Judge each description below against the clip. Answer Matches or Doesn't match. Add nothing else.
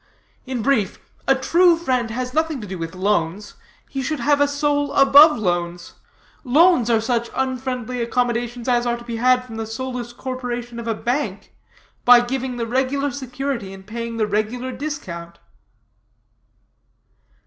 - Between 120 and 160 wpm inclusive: Matches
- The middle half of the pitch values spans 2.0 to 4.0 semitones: Matches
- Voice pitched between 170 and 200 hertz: Doesn't match